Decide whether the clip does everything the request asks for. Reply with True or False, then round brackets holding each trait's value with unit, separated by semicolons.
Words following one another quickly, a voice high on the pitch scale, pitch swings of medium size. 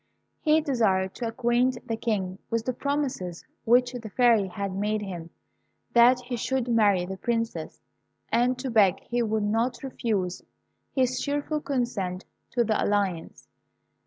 False (145 wpm; 230 Hz; 3.9 semitones)